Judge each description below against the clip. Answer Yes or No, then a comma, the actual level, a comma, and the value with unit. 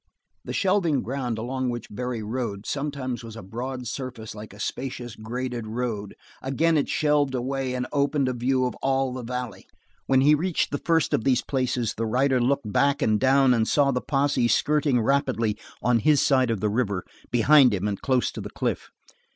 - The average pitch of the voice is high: No, low, 125 Hz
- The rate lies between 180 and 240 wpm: Yes, average, 190 wpm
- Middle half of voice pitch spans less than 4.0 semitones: Yes, average, 3.1 semitones